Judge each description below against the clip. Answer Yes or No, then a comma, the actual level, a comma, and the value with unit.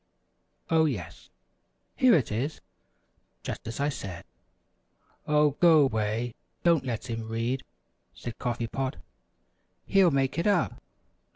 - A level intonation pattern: No, wide, 5.4 semitones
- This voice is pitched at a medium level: No, low, 130 Hz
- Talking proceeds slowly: Yes, slow, 120 wpm